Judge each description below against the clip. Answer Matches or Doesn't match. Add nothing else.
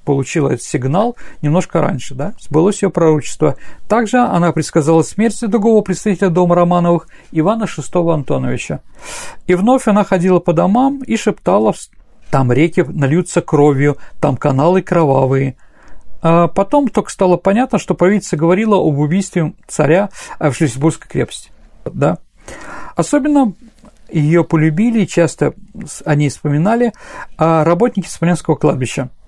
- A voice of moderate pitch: Matches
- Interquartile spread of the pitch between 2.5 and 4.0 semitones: Doesn't match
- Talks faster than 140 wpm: Doesn't match